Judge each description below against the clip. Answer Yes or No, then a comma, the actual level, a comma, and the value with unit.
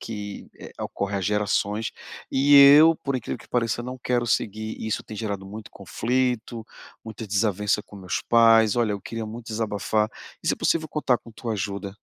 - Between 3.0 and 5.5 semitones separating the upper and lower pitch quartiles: No, narrow, 2.6 semitones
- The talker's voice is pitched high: No, low, 110 Hz